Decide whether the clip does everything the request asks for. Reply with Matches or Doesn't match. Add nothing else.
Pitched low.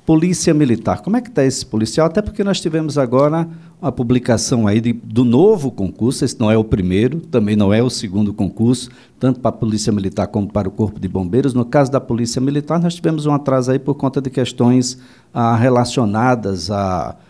Matches